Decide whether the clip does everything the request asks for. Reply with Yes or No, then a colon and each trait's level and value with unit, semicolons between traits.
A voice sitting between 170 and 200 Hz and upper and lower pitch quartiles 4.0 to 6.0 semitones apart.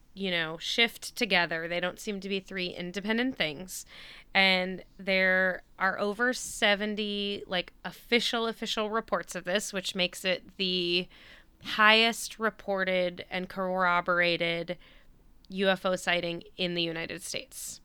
No: high, 190 Hz; narrow, 2.6 semitones